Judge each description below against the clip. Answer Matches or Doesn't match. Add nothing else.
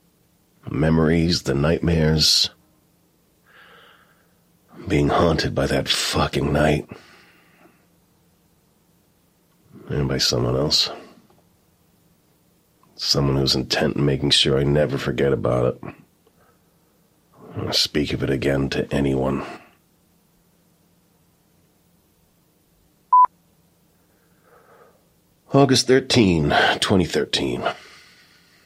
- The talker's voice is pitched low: Matches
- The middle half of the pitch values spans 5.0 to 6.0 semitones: Doesn't match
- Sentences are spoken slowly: Matches